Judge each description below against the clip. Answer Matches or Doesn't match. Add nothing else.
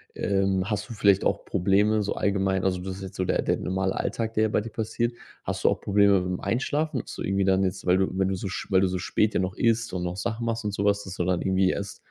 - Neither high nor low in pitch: Doesn't match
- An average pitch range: Doesn't match